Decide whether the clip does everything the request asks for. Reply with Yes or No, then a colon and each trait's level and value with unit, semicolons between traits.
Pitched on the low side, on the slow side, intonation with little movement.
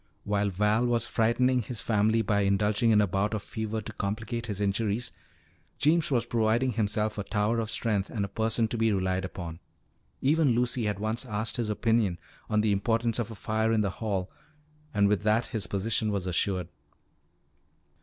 No: low, 110 Hz; average, 185 wpm; narrow, 2.2 semitones